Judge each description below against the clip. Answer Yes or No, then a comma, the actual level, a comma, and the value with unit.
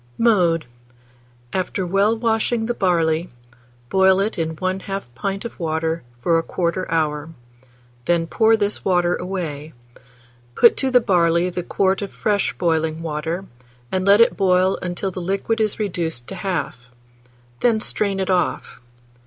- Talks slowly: No, average, 145 wpm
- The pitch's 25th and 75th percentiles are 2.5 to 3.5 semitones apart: Yes, average, 3.2 semitones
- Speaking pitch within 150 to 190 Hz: Yes, medium, 185 Hz